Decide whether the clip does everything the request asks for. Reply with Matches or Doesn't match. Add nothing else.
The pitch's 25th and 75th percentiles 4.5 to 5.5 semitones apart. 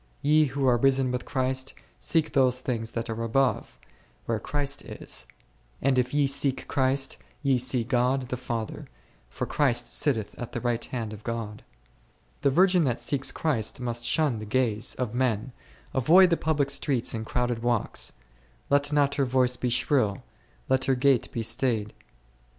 Doesn't match